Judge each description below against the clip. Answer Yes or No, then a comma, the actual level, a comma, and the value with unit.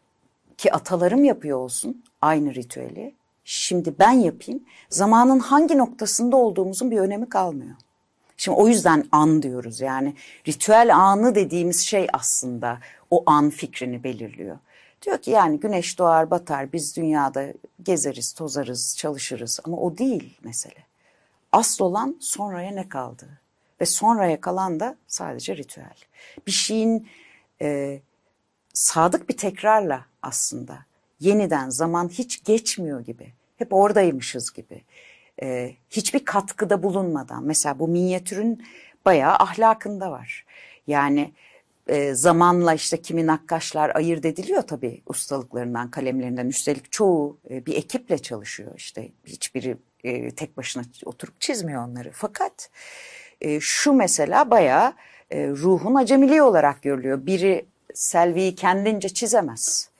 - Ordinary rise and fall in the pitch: No, wide, 6.8 semitones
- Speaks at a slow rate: No, average, 120 wpm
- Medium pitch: Yes, medium, 170 Hz